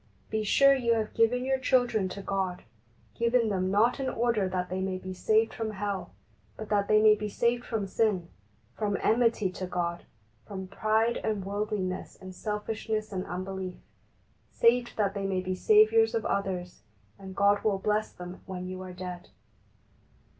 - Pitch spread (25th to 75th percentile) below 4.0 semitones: Yes, average, 3.2 semitones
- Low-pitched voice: No, high, 205 Hz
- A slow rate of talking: No, average, 175 wpm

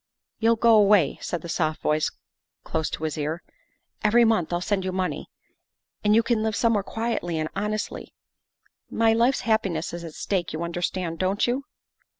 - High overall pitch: Yes, high, 195 Hz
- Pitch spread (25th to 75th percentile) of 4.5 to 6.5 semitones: Yes, average, 4.8 semitones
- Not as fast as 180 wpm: No, average, 185 wpm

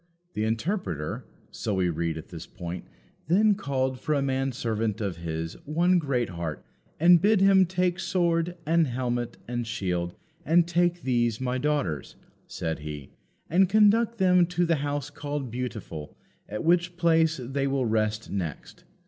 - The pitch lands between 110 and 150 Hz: Yes, low, 135 Hz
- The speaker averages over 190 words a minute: No, average, 155 wpm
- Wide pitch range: Yes, wide, 8.4 semitones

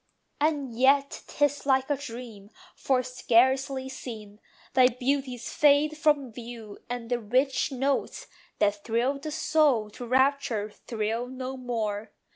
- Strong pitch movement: No, average, 3.2 semitones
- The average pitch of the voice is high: Yes, very high, 255 Hz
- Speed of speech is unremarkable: No, slow, 130 wpm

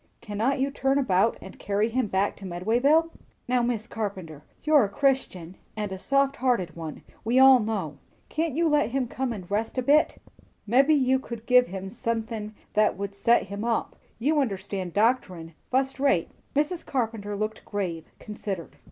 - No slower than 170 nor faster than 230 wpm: Yes, average, 175 wpm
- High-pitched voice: Yes, high, 225 Hz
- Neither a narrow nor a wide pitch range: Yes, average, 5.0 semitones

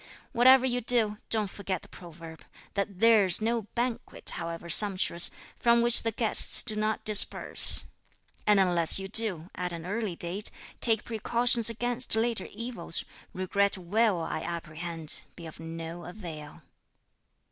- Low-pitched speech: No, high, 205 Hz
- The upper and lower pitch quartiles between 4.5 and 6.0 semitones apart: Yes, average, 5.0 semitones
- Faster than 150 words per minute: No, average, 140 wpm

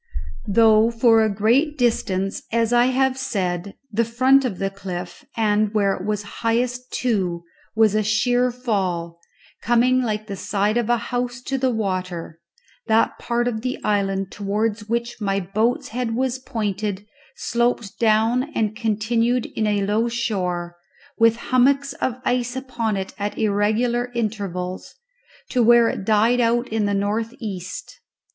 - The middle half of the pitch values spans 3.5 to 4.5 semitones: No, average, 3.0 semitones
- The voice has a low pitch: No, high, 220 Hz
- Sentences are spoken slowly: No, average, 150 wpm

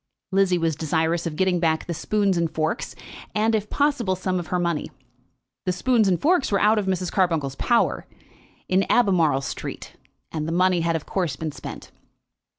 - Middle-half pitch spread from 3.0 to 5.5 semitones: Yes, average, 3.5 semitones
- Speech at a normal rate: Yes, average, 180 wpm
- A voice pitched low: No, medium, 180 Hz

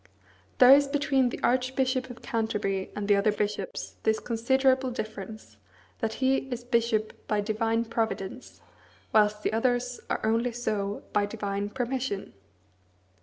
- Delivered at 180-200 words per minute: No, slow, 135 wpm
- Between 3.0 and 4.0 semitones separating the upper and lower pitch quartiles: Yes, average, 3.3 semitones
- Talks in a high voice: Yes, high, 230 Hz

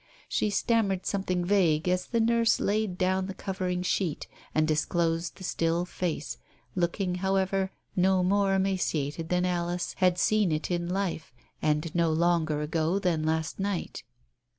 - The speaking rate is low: No, average, 150 wpm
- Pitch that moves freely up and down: No, average, 2.7 semitones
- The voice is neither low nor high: Yes, medium, 180 Hz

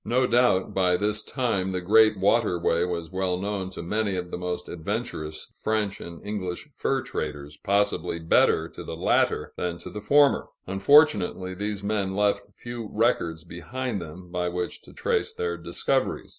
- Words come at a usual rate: Yes, average, 165 wpm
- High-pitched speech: No, very low, 95 Hz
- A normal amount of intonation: Yes, average, 3.6 semitones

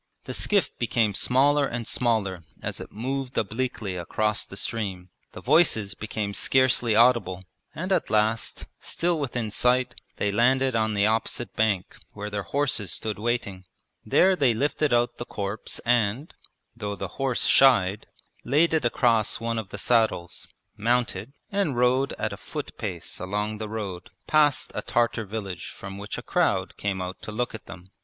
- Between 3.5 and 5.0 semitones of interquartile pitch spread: Yes, average, 3.8 semitones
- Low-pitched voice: Yes, low, 115 Hz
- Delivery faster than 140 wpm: Yes, average, 165 wpm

